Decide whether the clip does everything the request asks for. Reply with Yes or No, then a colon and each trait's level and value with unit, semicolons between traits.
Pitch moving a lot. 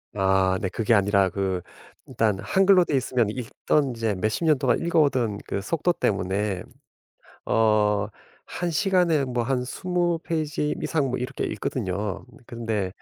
Yes: wide, 7.0 semitones